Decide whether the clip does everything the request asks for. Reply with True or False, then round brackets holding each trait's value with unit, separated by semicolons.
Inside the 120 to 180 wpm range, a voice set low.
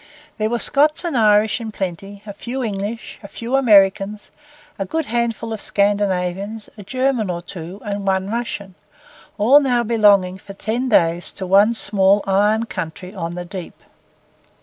False (160 wpm; 205 Hz)